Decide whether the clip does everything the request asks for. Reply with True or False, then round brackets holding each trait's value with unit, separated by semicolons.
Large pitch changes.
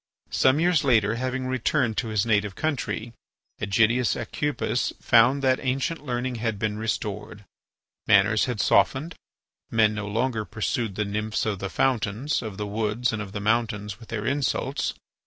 False (3.6 semitones)